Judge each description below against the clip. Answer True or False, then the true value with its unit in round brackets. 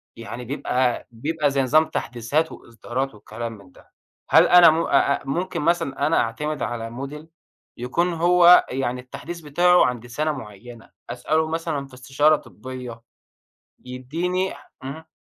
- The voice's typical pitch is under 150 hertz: True (140 Hz)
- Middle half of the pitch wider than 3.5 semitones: True (4.8 semitones)